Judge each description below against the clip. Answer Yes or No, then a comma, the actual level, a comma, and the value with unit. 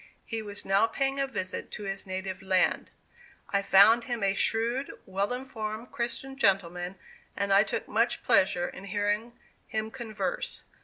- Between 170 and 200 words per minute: No, average, 155 wpm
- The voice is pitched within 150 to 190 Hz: No, high, 210 Hz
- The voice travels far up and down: No, average, 3.5 semitones